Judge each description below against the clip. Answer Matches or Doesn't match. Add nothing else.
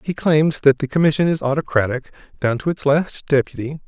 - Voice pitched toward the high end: Doesn't match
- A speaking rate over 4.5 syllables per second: Matches